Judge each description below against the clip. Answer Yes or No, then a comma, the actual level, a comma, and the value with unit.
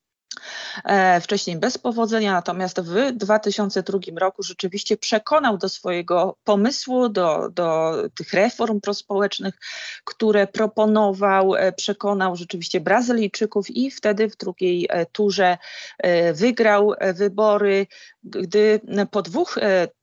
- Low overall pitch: No, high, 205 Hz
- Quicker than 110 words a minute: No, slow, 95 wpm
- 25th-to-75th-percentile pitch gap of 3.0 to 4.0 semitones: No, narrow, 2.6 semitones